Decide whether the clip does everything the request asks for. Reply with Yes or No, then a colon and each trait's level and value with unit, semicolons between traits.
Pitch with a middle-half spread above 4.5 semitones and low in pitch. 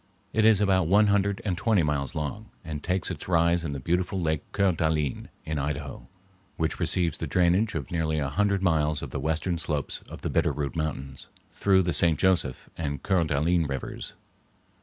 No: average, 4.0 semitones; very low, 80 Hz